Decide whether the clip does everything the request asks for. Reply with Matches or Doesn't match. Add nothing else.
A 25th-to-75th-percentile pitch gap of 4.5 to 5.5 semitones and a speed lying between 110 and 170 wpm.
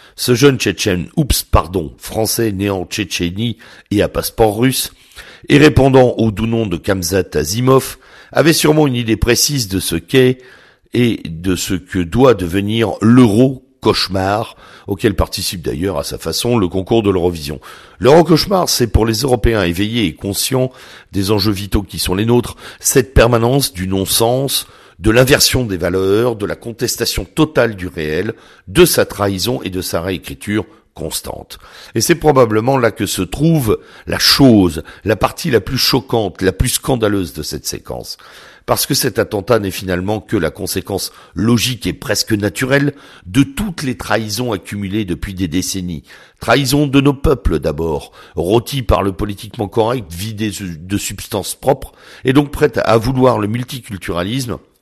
Matches